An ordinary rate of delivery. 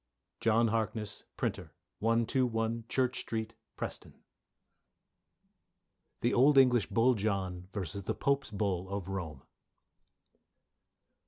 No: slow, 95 wpm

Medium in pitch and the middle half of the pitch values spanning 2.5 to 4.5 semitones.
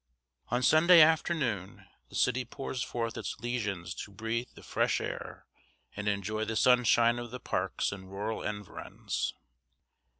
No: low, 115 Hz; average, 3.3 semitones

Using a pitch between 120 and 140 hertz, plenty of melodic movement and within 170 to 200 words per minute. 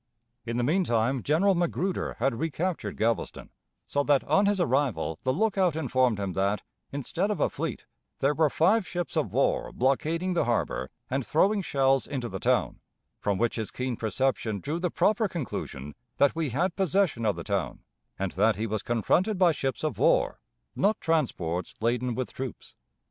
Yes: low, 135 Hz; wide, 7.0 semitones; average, 175 wpm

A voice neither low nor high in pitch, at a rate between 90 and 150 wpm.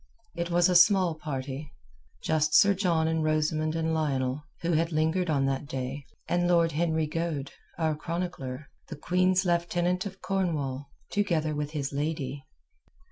Yes: medium, 160 Hz; average, 140 wpm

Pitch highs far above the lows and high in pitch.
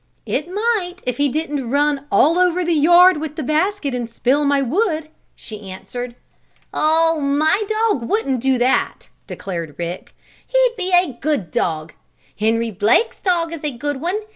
Yes: wide, 6.3 semitones; very high, 295 Hz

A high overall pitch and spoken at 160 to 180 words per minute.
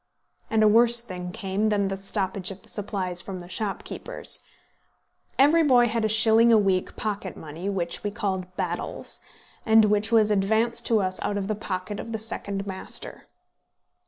Yes: high, 205 Hz; average, 175 wpm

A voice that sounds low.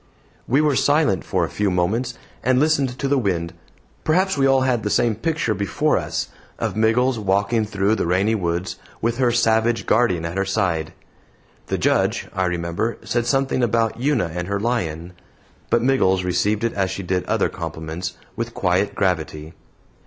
Yes: low, 110 Hz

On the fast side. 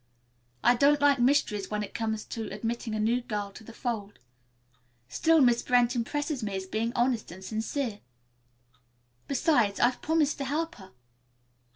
No: average, 160 wpm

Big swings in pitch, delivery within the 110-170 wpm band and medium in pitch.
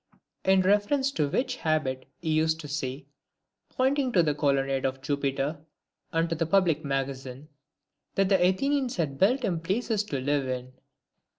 Yes: wide, 6.2 semitones; average, 165 wpm; medium, 160 Hz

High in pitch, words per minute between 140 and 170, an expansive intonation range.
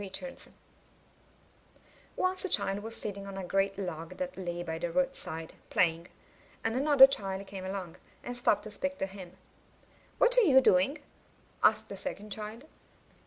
Yes: high, 200 Hz; average, 160 wpm; wide, 6.2 semitones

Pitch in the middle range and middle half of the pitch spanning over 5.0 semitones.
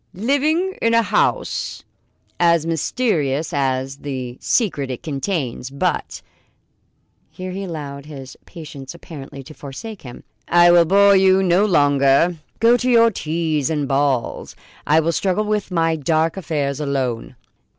Yes: medium, 160 Hz; wide, 5.5 semitones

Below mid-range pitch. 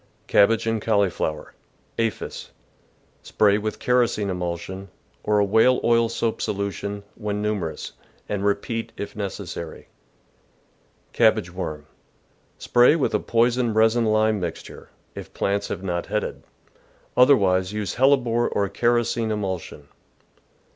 Yes: low, 105 Hz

